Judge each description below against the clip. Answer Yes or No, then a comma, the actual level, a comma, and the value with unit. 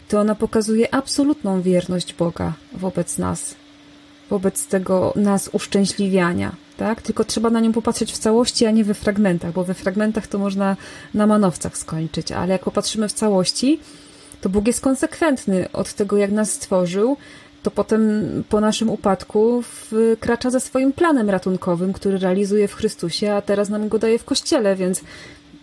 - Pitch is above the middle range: Yes, high, 210 Hz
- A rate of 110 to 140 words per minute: No, fast, 160 wpm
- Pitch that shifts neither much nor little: Yes, average, 3.1 semitones